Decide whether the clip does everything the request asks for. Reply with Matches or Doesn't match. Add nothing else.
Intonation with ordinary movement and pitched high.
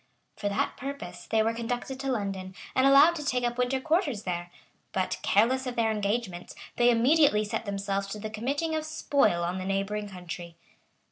Matches